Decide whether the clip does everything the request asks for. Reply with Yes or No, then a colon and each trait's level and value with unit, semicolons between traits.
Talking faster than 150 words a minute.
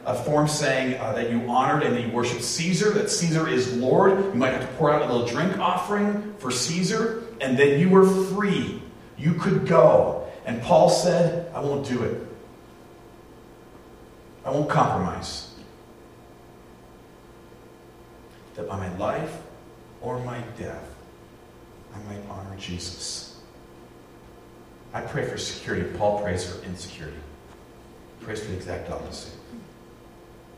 No: average, 140 wpm